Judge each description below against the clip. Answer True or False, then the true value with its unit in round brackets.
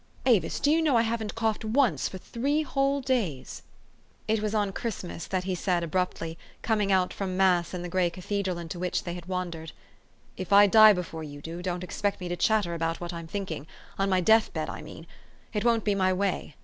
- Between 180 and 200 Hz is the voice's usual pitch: True (190 Hz)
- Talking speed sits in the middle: False (215 wpm)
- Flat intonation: False (3.9 semitones)